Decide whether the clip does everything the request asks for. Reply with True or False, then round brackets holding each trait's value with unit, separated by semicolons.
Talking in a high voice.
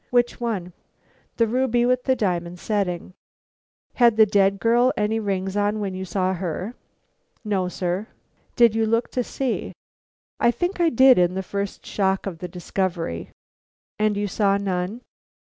True (205 Hz)